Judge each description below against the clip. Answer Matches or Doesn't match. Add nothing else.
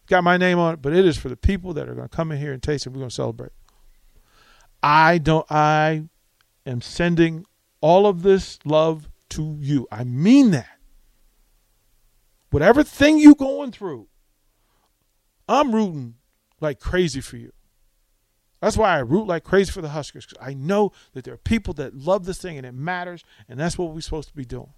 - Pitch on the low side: Doesn't match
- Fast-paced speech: Doesn't match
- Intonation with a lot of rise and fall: Matches